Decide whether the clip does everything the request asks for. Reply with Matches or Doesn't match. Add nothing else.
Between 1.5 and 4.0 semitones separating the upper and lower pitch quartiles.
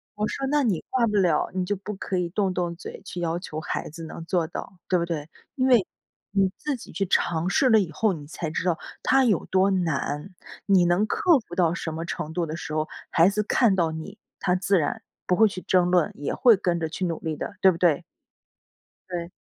Matches